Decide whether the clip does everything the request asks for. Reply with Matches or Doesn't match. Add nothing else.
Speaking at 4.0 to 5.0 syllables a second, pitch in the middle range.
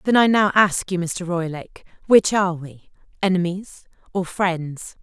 Matches